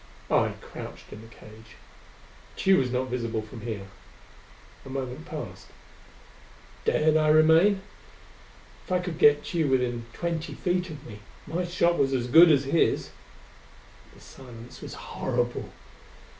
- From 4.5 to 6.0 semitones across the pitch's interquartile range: Yes, wide, 5.4 semitones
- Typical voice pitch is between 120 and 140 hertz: Yes, low, 135 Hz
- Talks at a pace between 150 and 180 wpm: No, average, 140 wpm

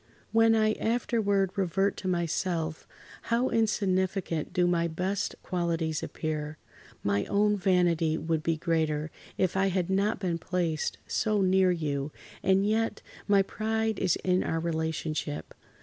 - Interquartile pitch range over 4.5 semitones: No, average, 3.7 semitones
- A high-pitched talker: No, medium, 180 Hz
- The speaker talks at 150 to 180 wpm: No, slow, 135 wpm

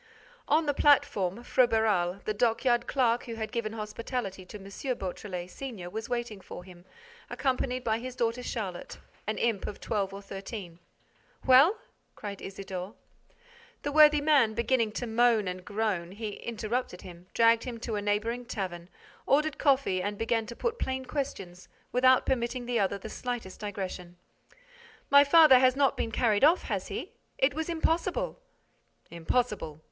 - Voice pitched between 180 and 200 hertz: No, high, 225 Hz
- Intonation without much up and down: No, average, 4.5 semitones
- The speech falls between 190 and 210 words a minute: No, average, 155 wpm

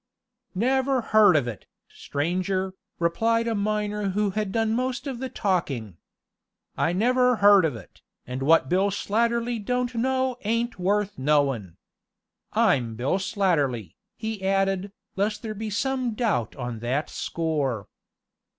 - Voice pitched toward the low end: No, high, 200 Hz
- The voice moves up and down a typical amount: No, wide, 7.2 semitones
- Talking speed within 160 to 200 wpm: No, slow, 135 wpm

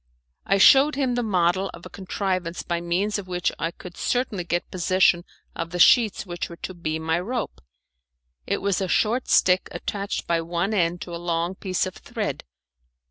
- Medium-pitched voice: Yes, medium, 180 Hz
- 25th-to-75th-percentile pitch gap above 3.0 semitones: No, average, 2.7 semitones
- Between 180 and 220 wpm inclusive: Yes, average, 190 wpm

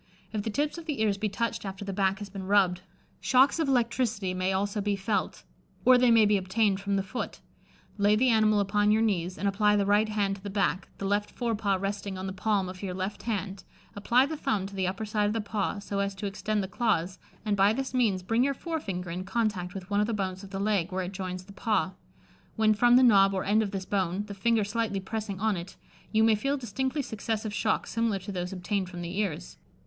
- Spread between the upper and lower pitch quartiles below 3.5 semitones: Yes, narrow, 2.4 semitones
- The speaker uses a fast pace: Yes, fast, 245 wpm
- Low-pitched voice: No, high, 205 Hz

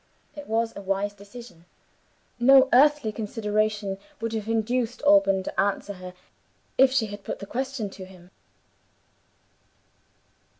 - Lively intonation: No, average, 3.7 semitones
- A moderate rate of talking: No, slow, 130 wpm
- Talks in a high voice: Yes, high, 215 Hz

